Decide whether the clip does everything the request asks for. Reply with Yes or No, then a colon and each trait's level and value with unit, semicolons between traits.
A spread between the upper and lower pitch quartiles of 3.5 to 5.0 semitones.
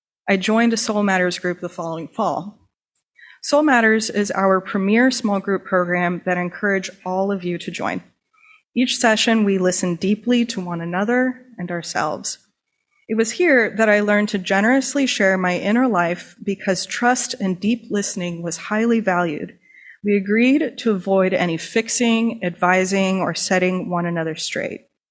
Yes: average, 4.0 semitones